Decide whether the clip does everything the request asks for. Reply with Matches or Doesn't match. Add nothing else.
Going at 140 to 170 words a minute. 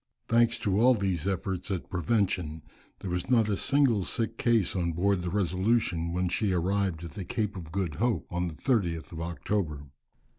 Doesn't match